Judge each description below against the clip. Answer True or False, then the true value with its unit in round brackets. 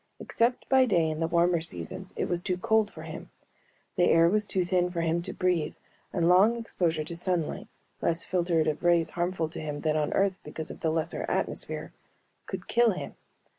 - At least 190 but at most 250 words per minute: True (200 wpm)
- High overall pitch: False (175 Hz)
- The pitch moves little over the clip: True (2.3 semitones)